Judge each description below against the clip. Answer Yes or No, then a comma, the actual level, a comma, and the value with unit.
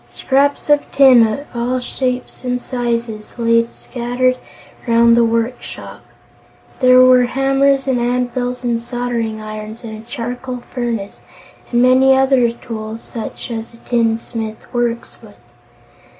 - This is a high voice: Yes, high, 240 Hz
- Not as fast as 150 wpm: Yes, slow, 135 wpm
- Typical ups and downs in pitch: No, narrow, 1.7 semitones